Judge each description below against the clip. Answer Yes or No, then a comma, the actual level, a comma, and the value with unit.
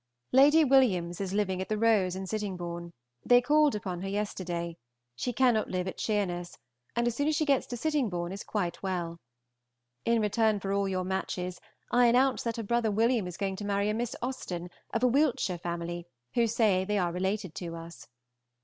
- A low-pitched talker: No, high, 200 Hz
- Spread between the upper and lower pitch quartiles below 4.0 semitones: No, average, 4.7 semitones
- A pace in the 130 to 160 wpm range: No, average, 195 wpm